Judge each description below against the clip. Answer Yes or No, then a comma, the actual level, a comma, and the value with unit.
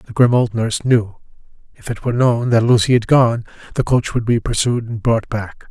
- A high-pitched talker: No, low, 115 Hz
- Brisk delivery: Yes, fast, 220 wpm